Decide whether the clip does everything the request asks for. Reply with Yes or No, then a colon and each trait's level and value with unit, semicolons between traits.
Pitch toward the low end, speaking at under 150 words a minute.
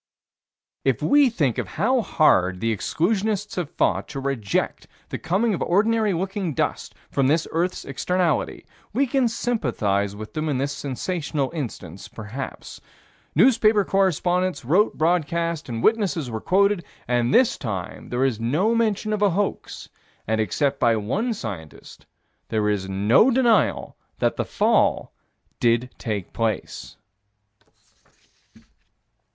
No: medium, 155 Hz; slow, 135 wpm